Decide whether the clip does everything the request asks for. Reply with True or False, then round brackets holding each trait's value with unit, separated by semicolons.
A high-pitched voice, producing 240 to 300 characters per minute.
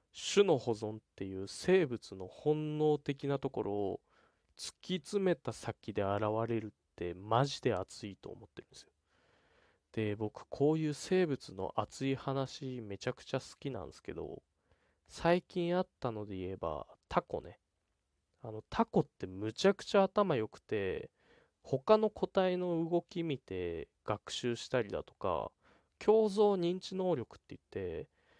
False (130 Hz; 270 characters per minute)